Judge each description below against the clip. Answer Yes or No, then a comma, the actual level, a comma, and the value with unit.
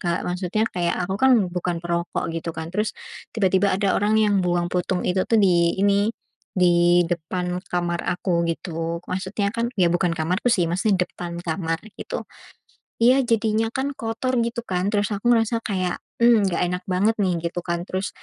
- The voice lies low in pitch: No, medium, 185 Hz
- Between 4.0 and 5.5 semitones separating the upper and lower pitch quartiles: No, average, 3.3 semitones